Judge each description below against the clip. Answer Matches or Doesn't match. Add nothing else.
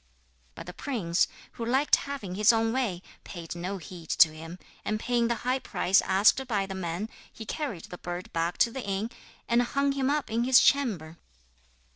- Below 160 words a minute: Doesn't match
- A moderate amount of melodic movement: Doesn't match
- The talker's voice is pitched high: Matches